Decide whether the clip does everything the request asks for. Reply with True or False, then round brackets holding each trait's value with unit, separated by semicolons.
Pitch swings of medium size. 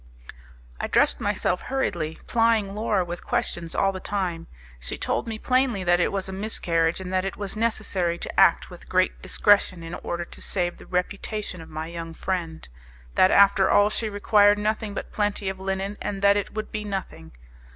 True (3.0 semitones)